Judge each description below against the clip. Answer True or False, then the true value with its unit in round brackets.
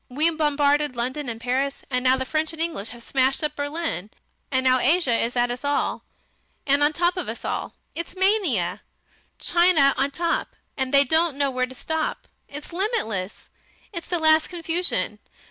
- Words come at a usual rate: True (185 wpm)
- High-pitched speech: True (285 Hz)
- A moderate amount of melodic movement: True (4.3 semitones)